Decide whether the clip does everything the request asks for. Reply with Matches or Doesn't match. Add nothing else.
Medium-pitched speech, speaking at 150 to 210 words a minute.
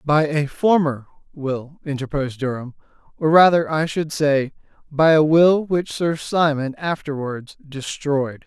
Doesn't match